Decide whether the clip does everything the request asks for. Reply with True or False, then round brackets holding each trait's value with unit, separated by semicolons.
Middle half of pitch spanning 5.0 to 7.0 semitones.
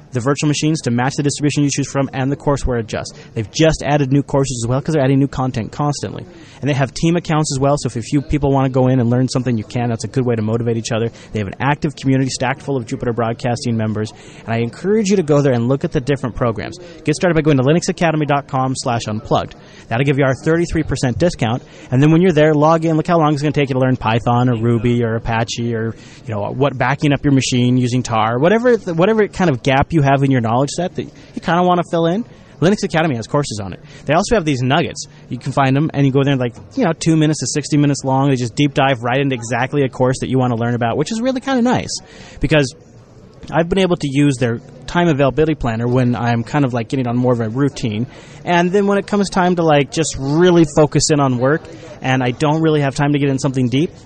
False (3.8 semitones)